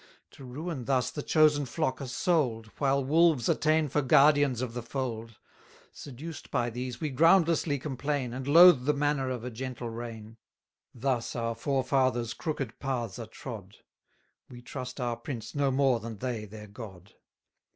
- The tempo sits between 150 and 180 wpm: Yes, average, 165 wpm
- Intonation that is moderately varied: Yes, average, 3.6 semitones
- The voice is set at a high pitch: No, low, 130 Hz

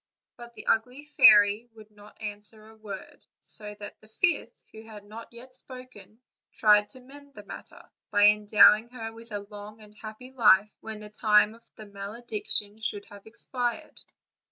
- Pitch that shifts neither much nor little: No, narrow, 2.3 semitones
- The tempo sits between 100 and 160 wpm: No, average, 170 wpm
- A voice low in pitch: No, high, 215 Hz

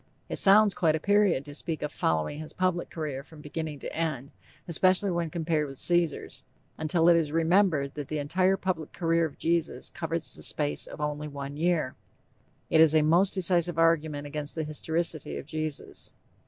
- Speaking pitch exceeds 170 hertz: No, medium, 160 Hz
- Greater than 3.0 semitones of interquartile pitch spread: No, narrow, 2.6 semitones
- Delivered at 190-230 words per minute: No, average, 180 wpm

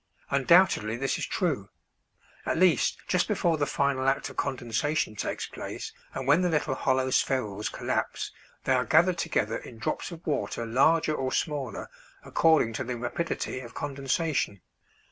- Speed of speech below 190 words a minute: Yes, average, 155 wpm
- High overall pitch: No, low, 135 Hz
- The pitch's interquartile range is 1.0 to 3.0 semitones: No, average, 4.5 semitones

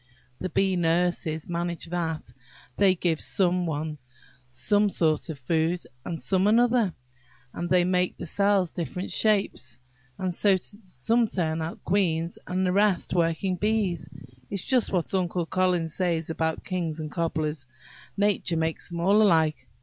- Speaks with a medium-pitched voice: Yes, medium, 175 Hz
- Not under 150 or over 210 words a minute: No, average, 140 wpm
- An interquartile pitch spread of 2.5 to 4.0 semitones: Yes, average, 3.0 semitones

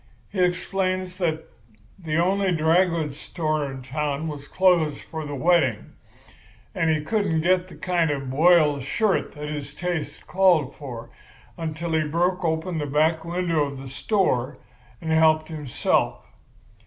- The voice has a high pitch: No, medium, 160 Hz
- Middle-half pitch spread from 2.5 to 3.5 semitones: Yes, average, 3.2 semitones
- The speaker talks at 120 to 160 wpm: Yes, average, 155 wpm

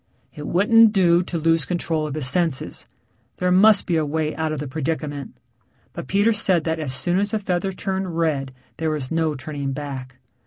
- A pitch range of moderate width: Yes, average, 3.6 semitones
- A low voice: No, medium, 160 Hz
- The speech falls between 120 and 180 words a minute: No, average, 195 wpm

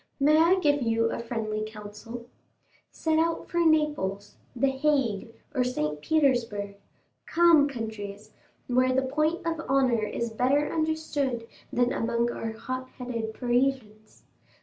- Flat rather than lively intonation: No, average, 4.8 semitones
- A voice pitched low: No, very high, 250 Hz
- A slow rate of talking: Yes, slow, 125 wpm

